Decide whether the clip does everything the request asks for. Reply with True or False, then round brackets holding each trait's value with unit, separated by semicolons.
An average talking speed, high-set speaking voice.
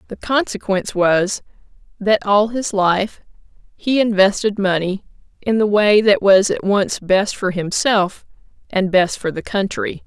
True (150 wpm; 200 Hz)